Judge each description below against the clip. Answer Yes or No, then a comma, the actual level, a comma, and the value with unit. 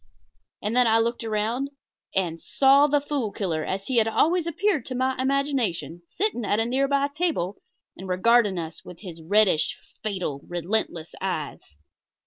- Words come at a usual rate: Yes, average, 155 wpm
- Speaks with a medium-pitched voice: No, high, 220 Hz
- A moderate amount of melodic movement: No, wide, 7.0 semitones